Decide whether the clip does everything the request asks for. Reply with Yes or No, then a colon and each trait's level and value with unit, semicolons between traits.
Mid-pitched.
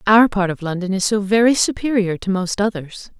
No: high, 200 Hz